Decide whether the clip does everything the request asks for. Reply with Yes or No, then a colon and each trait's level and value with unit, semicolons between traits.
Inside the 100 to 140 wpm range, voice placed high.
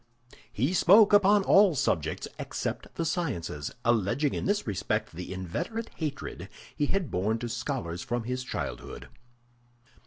No: slow, 135 wpm; low, 130 Hz